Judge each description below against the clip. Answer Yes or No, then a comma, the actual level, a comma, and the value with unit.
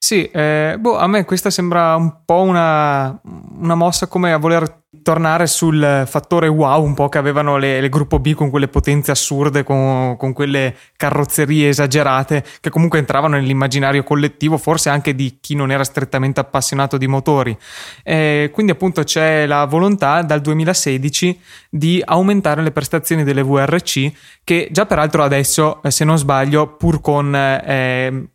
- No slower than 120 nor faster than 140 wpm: No, average, 160 wpm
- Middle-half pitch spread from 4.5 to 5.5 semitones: No, average, 2.8 semitones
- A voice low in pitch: No, medium, 150 Hz